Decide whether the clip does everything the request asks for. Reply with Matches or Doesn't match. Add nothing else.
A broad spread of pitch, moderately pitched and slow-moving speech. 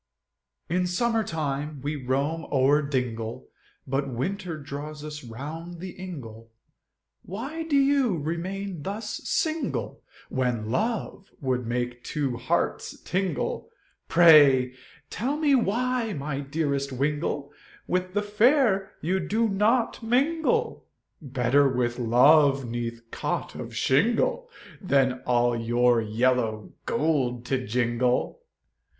Matches